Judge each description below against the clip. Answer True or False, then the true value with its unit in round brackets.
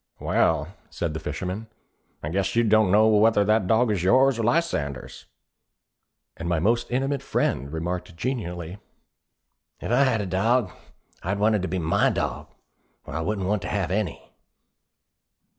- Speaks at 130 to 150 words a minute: False (160 wpm)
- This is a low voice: True (100 Hz)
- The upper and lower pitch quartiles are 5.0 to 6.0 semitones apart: False (4.4 semitones)